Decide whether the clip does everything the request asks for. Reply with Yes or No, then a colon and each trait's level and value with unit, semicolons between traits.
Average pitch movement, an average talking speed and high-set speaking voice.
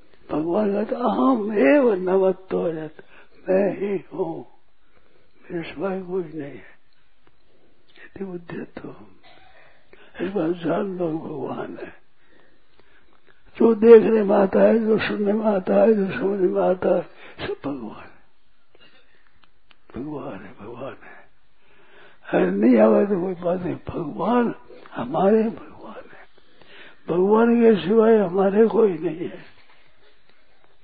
Yes: average, 3.5 semitones; average, 125 wpm; high, 195 Hz